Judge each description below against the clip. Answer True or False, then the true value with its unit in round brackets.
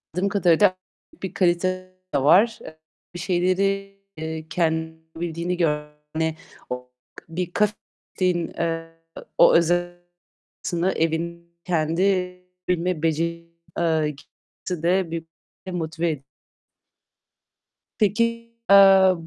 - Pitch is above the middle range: False (170 Hz)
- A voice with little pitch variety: True (2.2 semitones)